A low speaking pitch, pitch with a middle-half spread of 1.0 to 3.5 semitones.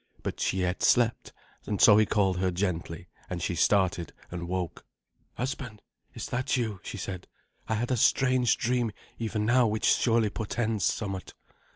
No: low, 105 Hz; average, 4.2 semitones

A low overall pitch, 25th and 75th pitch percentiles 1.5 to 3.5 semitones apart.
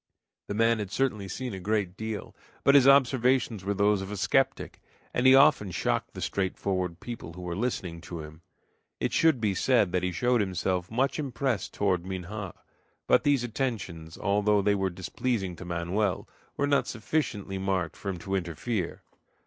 No: low, 100 Hz; average, 4.8 semitones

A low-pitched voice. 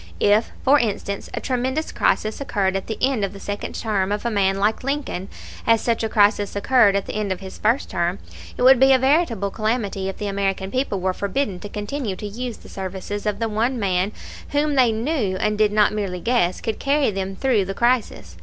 No: high, 210 Hz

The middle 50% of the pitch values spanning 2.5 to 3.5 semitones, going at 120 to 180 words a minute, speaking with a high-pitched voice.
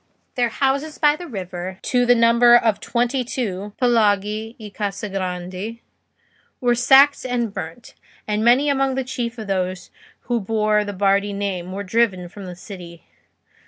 No: average, 3.9 semitones; average, 160 wpm; high, 220 Hz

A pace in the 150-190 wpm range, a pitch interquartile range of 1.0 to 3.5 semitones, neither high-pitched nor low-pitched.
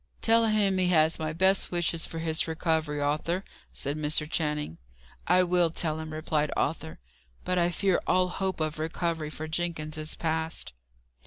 Yes: average, 165 wpm; narrow, 2.5 semitones; medium, 160 Hz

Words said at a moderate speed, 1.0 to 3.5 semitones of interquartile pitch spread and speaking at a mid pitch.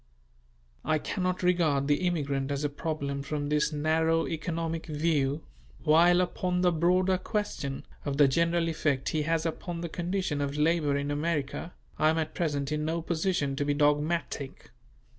Yes: average, 160 wpm; average, 2.7 semitones; medium, 155 Hz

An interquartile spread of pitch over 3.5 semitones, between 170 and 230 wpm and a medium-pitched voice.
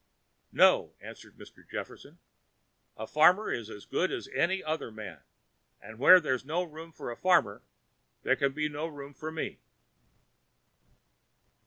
No: wide, 5.6 semitones; average, 145 wpm; medium, 150 Hz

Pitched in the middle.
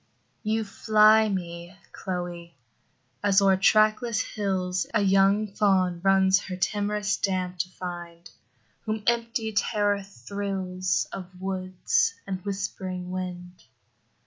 No: high, 195 Hz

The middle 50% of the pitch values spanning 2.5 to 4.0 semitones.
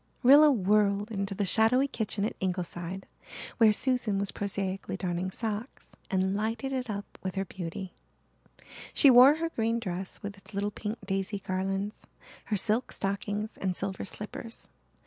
Yes: average, 2.8 semitones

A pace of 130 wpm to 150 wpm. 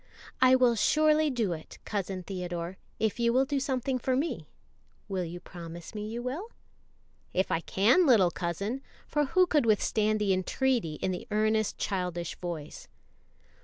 No: average, 160 wpm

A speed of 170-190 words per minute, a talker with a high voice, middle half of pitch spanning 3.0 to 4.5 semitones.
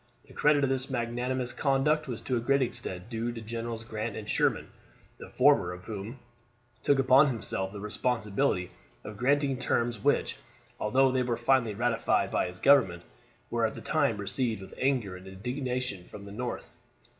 No: average, 175 wpm; low, 120 Hz; average, 3.7 semitones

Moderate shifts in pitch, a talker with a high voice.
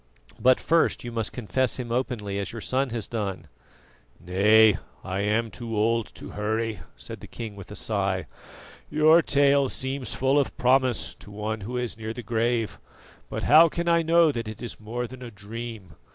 No: average, 3.6 semitones; low, 115 Hz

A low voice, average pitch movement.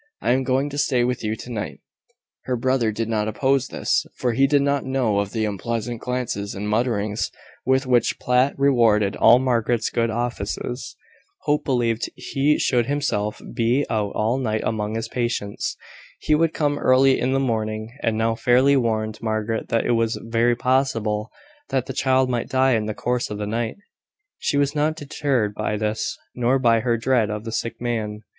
Yes: low, 120 Hz; average, 3.3 semitones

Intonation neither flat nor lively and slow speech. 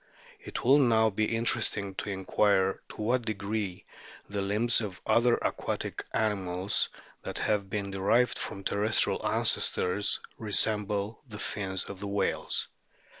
No: narrow, 2.2 semitones; slow, 130 wpm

